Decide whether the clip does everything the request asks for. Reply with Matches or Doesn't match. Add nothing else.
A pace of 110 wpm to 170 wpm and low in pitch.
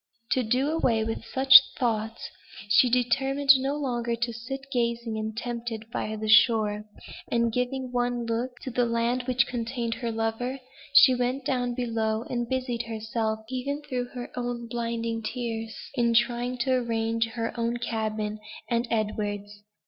Doesn't match